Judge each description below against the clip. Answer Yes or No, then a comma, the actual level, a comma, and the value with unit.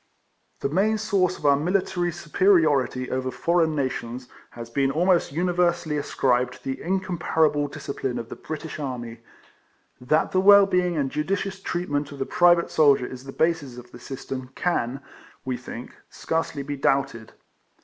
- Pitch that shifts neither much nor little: Yes, average, 5.0 semitones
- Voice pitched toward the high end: No, medium, 150 Hz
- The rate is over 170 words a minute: No, average, 160 wpm